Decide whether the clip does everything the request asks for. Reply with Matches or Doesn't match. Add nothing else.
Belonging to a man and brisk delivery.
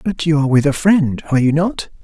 Matches